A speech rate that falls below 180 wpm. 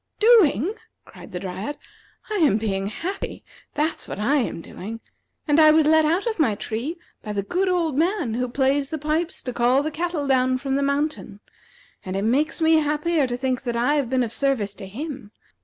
No: fast, 205 wpm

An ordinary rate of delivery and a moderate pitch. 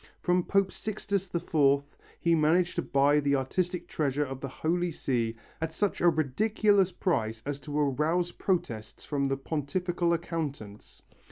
Yes: average, 150 wpm; medium, 155 Hz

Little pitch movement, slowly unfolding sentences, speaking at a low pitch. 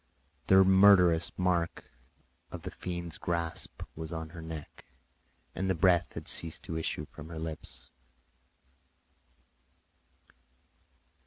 Yes: narrow, 2.0 semitones; slow, 110 wpm; very low, 85 Hz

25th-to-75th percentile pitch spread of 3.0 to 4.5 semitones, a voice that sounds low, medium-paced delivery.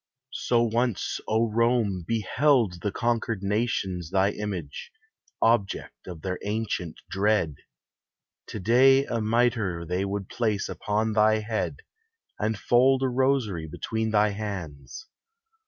No: average, 3.4 semitones; low, 110 Hz; slow, 120 wpm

